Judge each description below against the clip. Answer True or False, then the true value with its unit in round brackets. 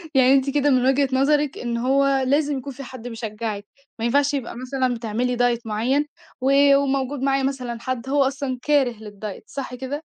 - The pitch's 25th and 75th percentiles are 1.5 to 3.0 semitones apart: True (2.4 semitones)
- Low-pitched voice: False (260 Hz)